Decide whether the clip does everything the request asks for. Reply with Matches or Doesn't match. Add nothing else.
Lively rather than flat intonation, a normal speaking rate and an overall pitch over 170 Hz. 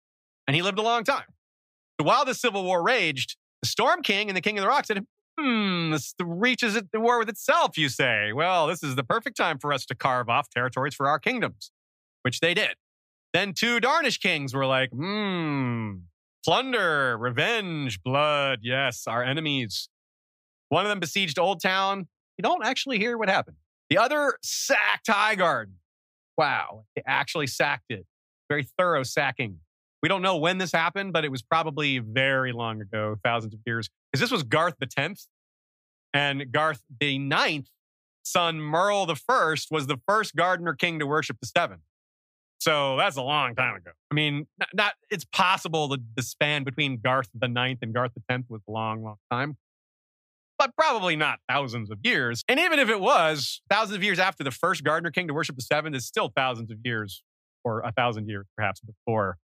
Doesn't match